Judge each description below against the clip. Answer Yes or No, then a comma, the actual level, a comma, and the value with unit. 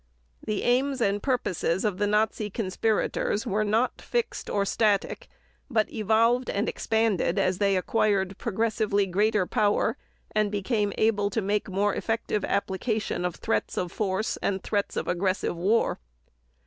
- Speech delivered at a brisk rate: No, average, 145 wpm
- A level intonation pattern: Yes, narrow, 2.3 semitones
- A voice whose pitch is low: No, high, 210 Hz